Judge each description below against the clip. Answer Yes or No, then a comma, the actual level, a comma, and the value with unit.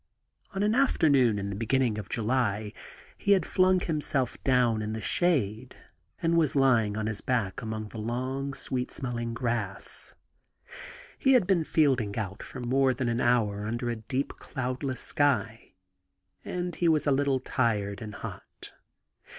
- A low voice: Yes, low, 125 Hz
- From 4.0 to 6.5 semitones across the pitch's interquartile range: Yes, average, 4.3 semitones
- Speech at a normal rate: Yes, average, 160 wpm